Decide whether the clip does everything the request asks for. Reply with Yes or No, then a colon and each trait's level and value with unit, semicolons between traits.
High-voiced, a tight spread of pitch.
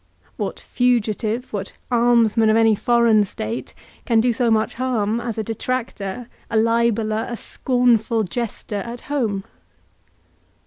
Yes: high, 230 Hz; narrow, 1.9 semitones